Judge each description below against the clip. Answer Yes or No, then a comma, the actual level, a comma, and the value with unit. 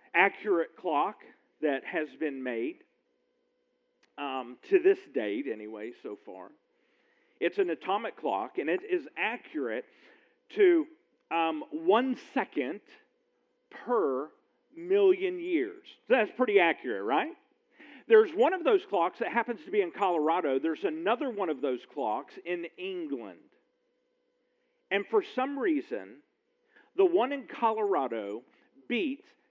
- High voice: Yes, very high, 375 Hz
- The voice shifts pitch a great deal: Yes, wide, 6.7 semitones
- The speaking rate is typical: No, slow, 125 wpm